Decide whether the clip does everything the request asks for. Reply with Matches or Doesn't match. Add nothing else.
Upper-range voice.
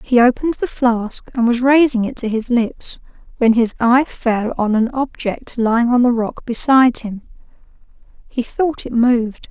Matches